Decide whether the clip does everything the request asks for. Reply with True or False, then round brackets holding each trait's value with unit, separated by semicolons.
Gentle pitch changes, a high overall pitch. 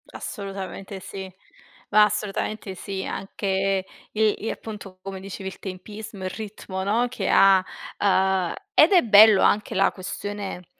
True (1.7 semitones; 195 Hz)